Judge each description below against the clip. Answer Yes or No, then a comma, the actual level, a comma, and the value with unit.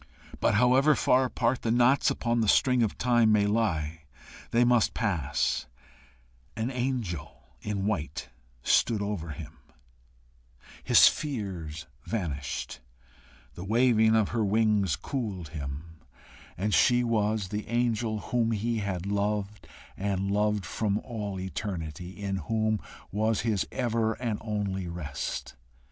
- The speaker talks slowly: Yes, slow, 125 wpm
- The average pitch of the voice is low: Yes, low, 105 Hz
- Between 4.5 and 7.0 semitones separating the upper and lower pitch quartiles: No, average, 3.8 semitones